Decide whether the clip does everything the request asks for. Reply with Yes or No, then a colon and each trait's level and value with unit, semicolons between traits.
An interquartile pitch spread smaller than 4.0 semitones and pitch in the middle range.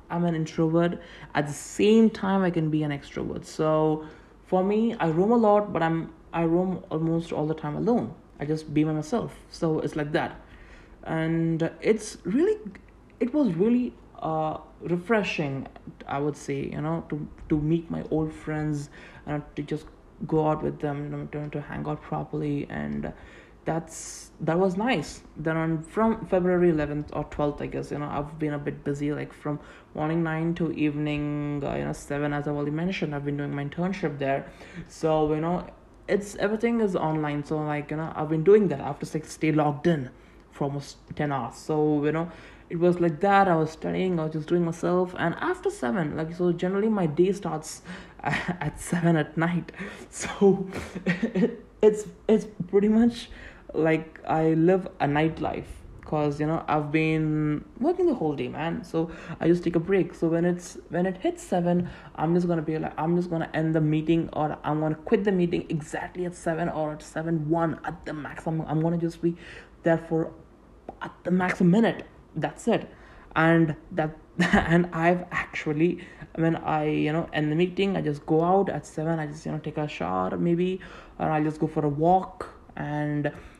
Yes: average, 2.7 semitones; medium, 160 Hz